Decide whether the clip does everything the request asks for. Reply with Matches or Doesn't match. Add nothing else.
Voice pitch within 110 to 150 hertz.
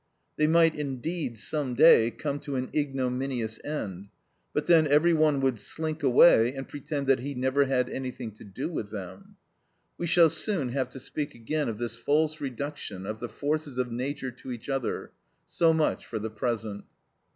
Matches